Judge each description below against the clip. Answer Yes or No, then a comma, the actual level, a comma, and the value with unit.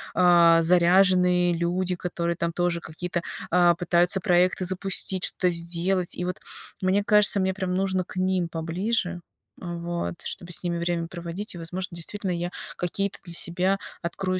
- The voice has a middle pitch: Yes, medium, 180 Hz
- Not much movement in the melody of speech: Yes, narrow, 1.5 semitones